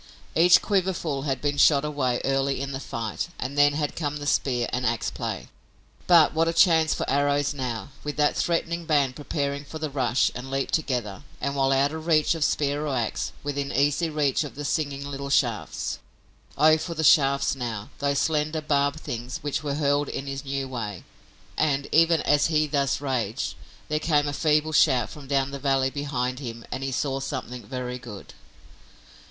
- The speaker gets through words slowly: No, average, 190 wpm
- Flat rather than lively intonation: Yes, narrow, 2.2 semitones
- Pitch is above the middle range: No, medium, 140 Hz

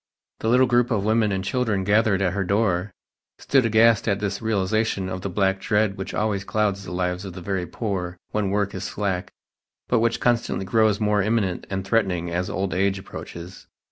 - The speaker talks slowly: No, average, 195 wpm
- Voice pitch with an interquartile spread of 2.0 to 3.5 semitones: Yes, narrow, 2.6 semitones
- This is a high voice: No, low, 100 Hz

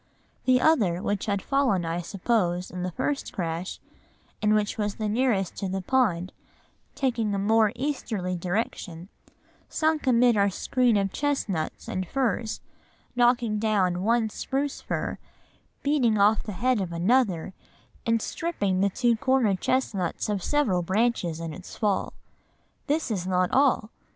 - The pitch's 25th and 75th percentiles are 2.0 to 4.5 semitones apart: No, average, 5.1 semitones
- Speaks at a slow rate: No, average, 145 wpm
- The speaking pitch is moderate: No, high, 210 Hz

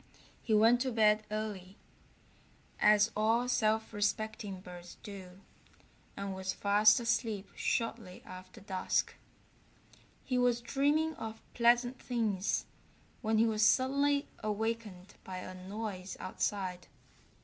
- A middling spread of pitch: Yes, average, 3.3 semitones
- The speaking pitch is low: No, high, 215 Hz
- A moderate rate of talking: No, slow, 115 wpm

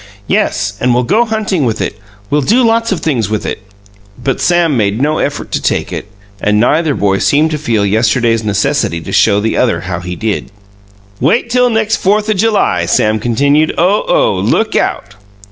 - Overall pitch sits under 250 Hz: Yes, medium, 140 Hz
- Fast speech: No, average, 190 wpm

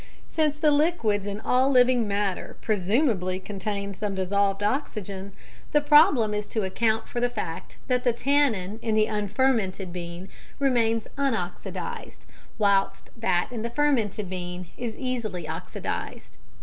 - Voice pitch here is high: Yes, high, 215 Hz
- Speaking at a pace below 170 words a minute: Yes, slow, 135 wpm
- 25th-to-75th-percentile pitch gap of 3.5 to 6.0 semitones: Yes, average, 4.5 semitones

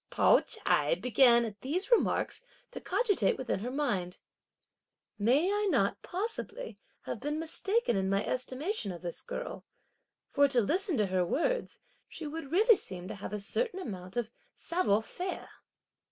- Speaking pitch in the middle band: No, very high, 265 Hz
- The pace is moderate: Yes, average, 155 wpm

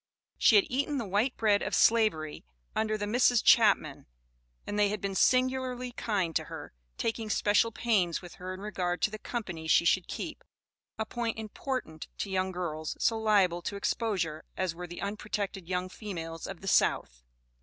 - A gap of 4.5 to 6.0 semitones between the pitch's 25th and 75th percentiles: No, average, 4.1 semitones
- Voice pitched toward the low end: No, high, 205 Hz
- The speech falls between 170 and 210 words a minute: Yes, average, 175 wpm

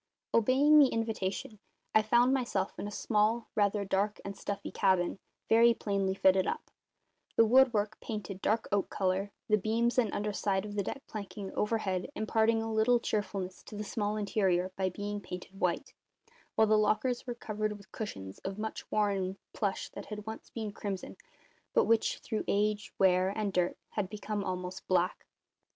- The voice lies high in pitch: Yes, high, 210 Hz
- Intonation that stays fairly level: Yes, narrow, 2.3 semitones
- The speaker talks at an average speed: Yes, average, 170 wpm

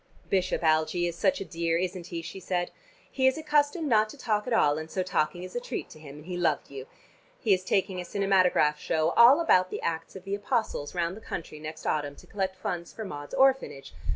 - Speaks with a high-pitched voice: No, medium, 180 Hz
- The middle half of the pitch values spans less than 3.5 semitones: No, average, 4.3 semitones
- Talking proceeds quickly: Yes, fast, 230 wpm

